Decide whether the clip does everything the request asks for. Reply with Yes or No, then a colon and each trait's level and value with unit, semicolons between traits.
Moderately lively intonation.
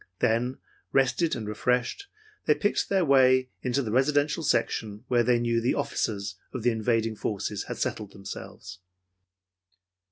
Yes: average, 3.5 semitones